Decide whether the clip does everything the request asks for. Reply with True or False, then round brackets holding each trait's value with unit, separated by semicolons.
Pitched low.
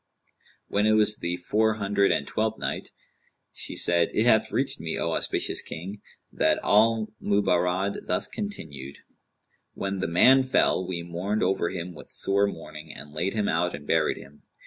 True (95 Hz)